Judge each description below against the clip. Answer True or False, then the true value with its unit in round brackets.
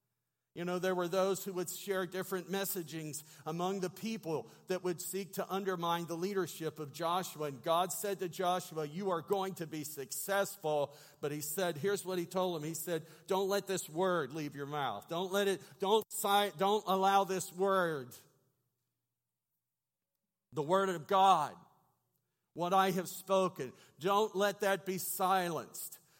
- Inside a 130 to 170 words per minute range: True (165 wpm)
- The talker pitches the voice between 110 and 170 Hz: False (180 Hz)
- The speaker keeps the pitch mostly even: False (3.3 semitones)